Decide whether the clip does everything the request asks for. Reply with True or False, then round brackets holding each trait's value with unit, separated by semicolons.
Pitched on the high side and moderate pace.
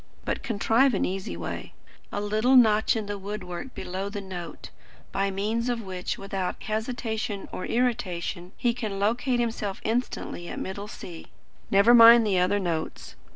True (205 Hz; 160 wpm)